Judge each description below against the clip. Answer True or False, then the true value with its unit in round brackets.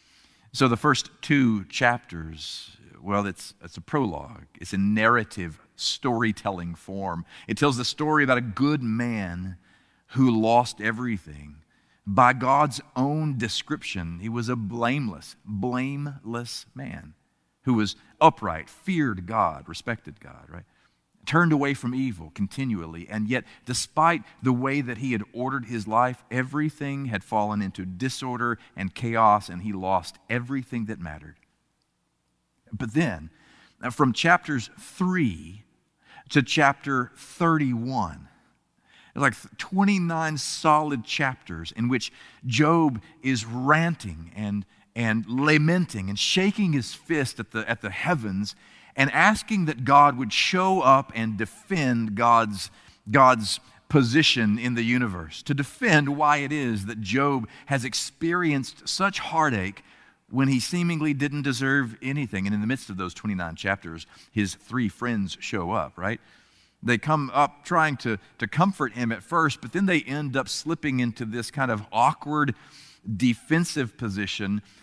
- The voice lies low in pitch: True (120 Hz)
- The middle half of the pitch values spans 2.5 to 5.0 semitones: False (5.6 semitones)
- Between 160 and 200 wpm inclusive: False (135 wpm)